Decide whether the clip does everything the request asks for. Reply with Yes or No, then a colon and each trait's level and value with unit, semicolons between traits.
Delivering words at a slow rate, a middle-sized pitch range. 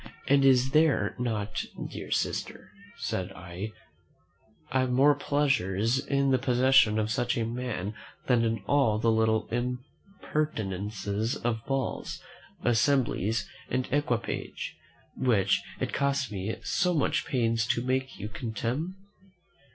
Yes: slow, 120 wpm; average, 3.7 semitones